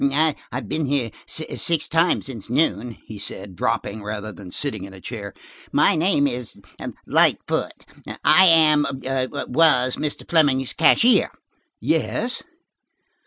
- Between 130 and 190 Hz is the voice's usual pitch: Yes, low, 135 Hz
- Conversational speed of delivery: No, slow, 120 wpm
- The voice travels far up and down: Yes, wide, 6.2 semitones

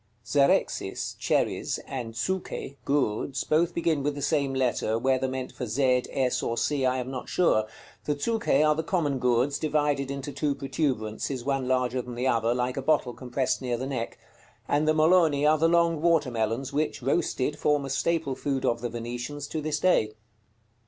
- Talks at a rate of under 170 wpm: No, average, 185 wpm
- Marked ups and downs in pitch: No, average, 3.2 semitones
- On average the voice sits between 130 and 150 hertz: Yes, low, 135 Hz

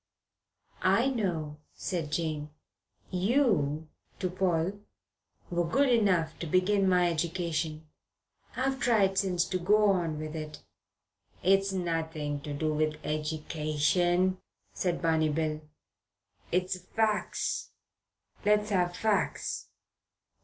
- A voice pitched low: No, medium, 175 Hz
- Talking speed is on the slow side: Yes, slow, 105 wpm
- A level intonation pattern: No, average, 3.8 semitones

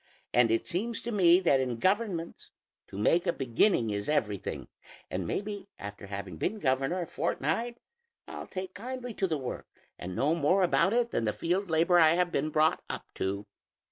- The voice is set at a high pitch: No, medium, 165 Hz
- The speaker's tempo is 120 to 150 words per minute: No, average, 185 wpm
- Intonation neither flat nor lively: No, wide, 8.5 semitones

